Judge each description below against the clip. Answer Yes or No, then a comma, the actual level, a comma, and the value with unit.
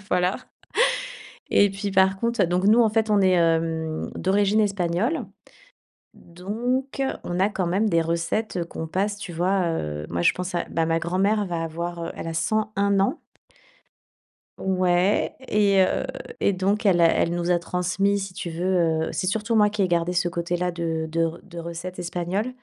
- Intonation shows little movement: No, average, 3.0 semitones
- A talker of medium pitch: Yes, medium, 180 Hz